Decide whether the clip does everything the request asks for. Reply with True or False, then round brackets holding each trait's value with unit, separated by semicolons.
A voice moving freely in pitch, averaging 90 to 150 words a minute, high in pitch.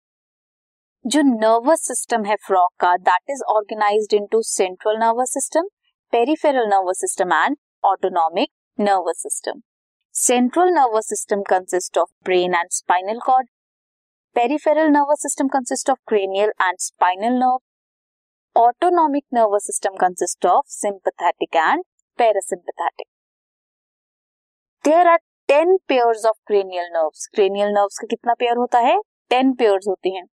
True (6.1 semitones; 130 wpm; 225 Hz)